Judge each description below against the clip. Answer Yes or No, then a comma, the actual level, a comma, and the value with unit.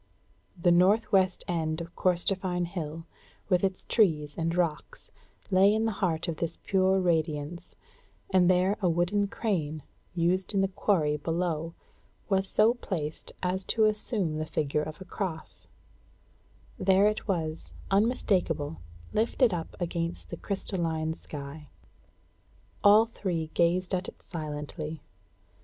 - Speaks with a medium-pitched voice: Yes, medium, 175 Hz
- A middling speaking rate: No, slow, 130 wpm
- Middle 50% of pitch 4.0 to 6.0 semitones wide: No, average, 3.4 semitones